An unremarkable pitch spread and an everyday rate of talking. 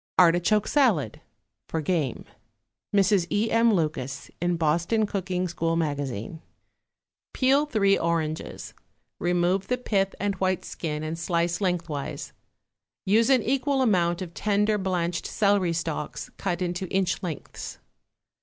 No: average, 3.6 semitones; slow, 125 wpm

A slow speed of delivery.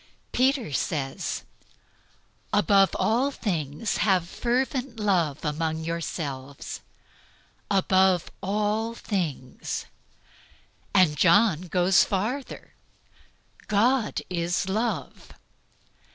Yes: slow, 75 wpm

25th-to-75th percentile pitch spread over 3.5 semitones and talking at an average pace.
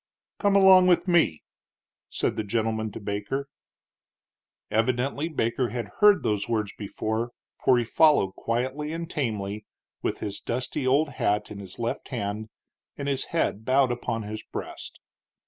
Yes: average, 5.0 semitones; average, 145 wpm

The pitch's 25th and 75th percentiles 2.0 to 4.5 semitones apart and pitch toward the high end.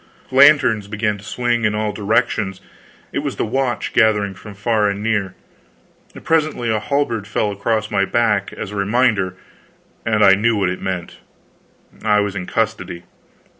No: average, 2.7 semitones; low, 105 Hz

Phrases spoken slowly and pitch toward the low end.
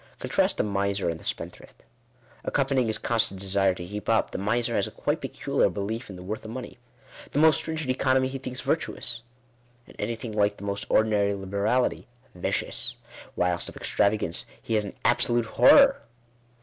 No: average, 175 wpm; low, 110 Hz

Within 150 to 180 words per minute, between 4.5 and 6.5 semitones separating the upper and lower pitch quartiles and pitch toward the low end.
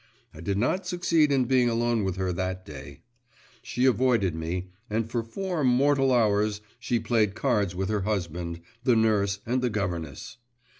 Yes: average, 165 wpm; average, 5.1 semitones; low, 110 Hz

